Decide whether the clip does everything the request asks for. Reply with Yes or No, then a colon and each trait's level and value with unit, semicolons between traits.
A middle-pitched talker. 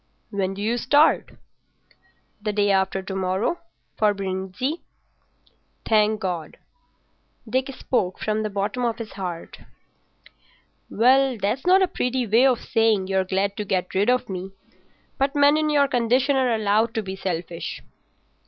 No: high, 215 Hz